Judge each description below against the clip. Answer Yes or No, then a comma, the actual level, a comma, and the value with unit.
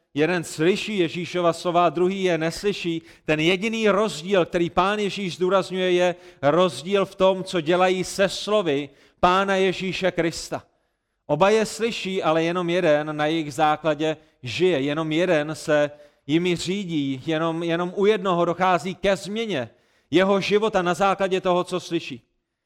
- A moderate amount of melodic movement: Yes, average, 3.1 semitones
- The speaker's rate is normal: Yes, average, 145 wpm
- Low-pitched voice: No, medium, 180 Hz